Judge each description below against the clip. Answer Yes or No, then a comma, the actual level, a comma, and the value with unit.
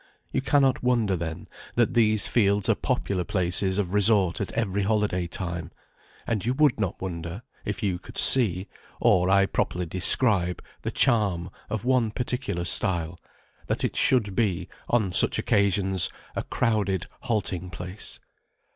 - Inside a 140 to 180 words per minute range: Yes, average, 145 wpm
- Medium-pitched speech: No, low, 100 Hz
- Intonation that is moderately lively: Yes, average, 3.7 semitones